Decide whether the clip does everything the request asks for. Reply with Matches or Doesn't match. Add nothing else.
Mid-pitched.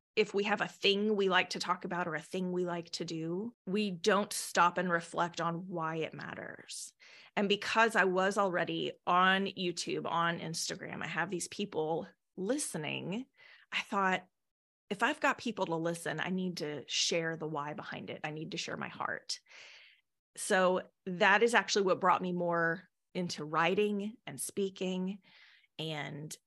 Matches